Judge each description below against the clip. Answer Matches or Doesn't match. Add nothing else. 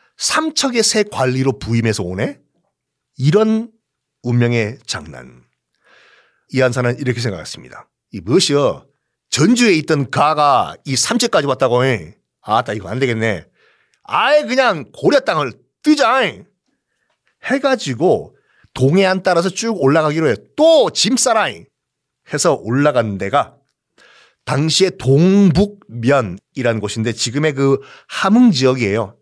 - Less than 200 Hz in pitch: Matches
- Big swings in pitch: Matches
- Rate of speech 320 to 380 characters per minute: Doesn't match